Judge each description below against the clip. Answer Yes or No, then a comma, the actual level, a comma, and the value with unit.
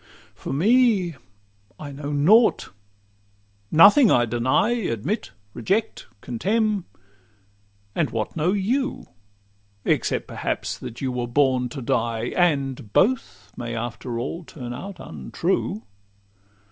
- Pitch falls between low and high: Yes, medium, 145 Hz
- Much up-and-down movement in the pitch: Yes, wide, 8.6 semitones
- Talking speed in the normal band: No, slow, 110 wpm